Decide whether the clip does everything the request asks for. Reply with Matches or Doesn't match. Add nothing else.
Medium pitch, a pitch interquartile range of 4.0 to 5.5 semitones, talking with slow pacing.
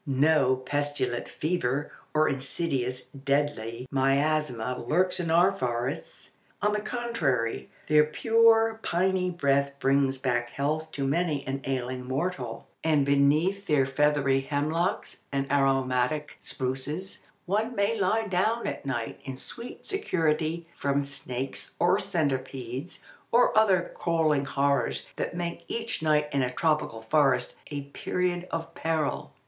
Matches